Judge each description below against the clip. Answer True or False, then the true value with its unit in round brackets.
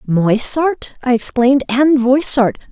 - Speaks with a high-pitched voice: True (255 Hz)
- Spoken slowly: True (110 wpm)